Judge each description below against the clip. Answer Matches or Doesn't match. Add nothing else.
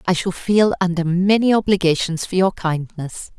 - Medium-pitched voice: Matches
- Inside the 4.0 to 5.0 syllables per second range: Matches